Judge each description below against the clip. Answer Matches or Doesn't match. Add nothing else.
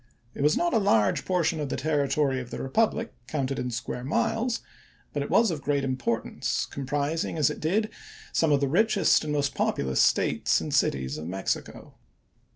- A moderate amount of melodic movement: Doesn't match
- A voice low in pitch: Doesn't match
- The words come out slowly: Doesn't match